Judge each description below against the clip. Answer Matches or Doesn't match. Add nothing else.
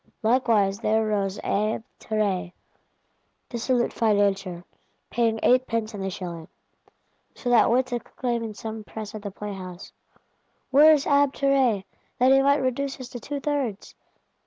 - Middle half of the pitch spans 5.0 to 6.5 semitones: Doesn't match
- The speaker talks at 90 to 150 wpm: Matches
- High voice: Matches